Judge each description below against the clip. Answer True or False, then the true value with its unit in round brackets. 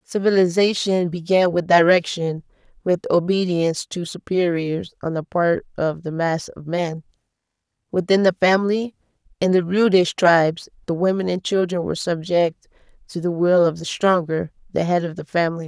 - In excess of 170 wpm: False (155 wpm)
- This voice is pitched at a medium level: True (175 Hz)